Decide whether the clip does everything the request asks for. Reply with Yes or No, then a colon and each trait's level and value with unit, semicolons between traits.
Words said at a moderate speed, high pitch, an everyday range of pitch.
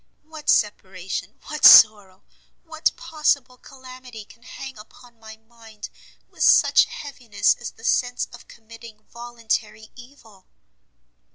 No: slow, 115 wpm; high, 235 Hz; average, 3.0 semitones